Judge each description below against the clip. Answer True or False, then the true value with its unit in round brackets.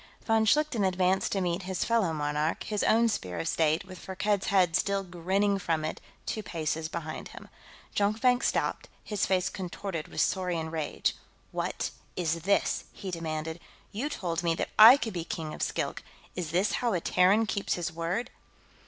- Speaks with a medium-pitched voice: True (180 Hz)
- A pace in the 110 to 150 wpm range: False (175 wpm)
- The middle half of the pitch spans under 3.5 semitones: False (3.8 semitones)